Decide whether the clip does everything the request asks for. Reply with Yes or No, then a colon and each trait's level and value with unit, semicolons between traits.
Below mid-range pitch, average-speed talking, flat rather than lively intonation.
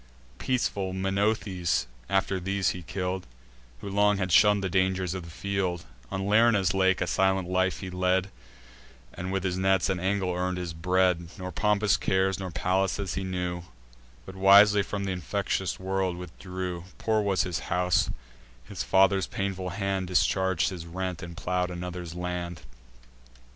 Yes: very low, 95 Hz; average, 155 wpm; narrow, 1.4 semitones